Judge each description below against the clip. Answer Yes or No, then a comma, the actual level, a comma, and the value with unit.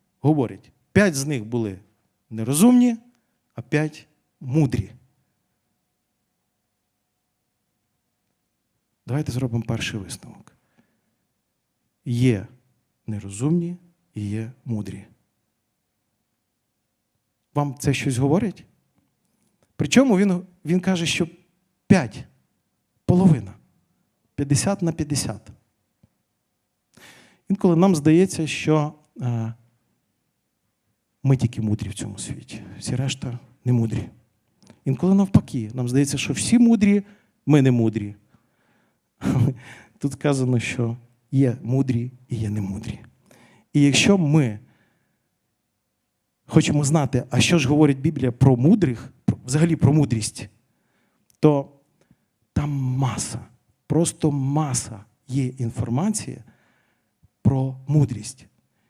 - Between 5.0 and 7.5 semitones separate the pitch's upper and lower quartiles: Yes, wide, 5.4 semitones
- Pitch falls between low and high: No, low, 130 Hz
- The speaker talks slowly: Yes, slow, 90 wpm